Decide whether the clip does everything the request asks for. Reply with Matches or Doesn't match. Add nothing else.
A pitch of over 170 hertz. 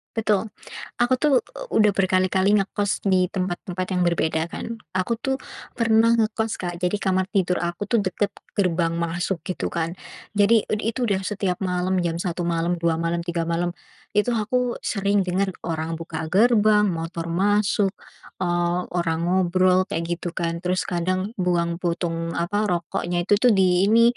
Matches